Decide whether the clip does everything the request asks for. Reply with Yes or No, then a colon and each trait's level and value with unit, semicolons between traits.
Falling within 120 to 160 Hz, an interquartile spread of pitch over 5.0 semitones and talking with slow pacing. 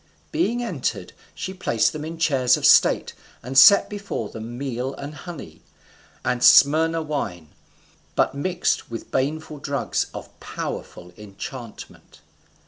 Yes: medium, 140 Hz; wide, 5.5 semitones; slow, 130 wpm